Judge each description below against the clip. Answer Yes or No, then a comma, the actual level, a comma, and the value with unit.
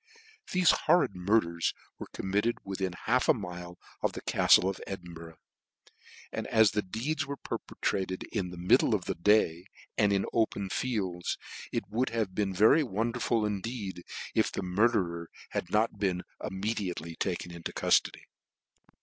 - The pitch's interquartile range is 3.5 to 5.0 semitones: Yes, average, 3.8 semitones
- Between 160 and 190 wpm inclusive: No, average, 150 wpm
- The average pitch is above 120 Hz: No, low, 100 Hz